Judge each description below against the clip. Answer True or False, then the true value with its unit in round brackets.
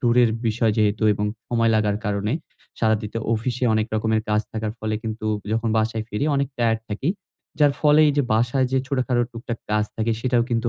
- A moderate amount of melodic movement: False (2.1 semitones)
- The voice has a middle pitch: False (115 Hz)